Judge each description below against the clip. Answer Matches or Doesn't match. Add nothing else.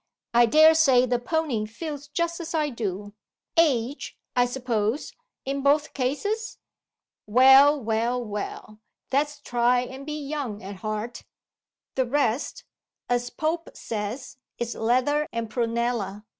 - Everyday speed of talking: Doesn't match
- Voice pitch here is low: Doesn't match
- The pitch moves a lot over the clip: Doesn't match